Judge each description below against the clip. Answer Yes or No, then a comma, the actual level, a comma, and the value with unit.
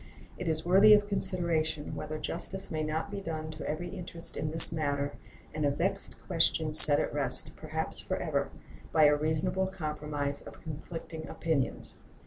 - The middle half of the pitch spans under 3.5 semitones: Yes, narrow, 2.5 semitones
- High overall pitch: No, medium, 160 Hz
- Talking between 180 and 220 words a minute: No, average, 160 wpm